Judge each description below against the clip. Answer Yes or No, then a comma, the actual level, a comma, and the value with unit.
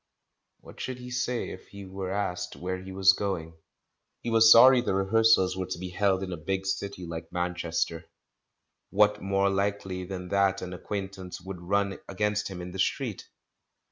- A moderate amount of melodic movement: No, narrow, 1.8 semitones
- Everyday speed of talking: Yes, average, 175 wpm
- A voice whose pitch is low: Yes, very low, 95 Hz